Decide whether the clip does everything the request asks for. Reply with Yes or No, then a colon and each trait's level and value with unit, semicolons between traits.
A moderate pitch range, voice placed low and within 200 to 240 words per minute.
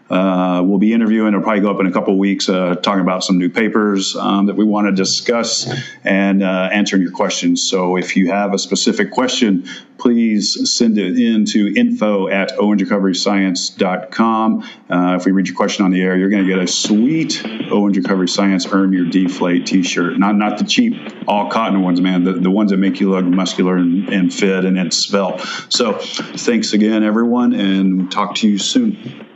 No: narrow, 2.3 semitones; low, 100 Hz; fast, 205 wpm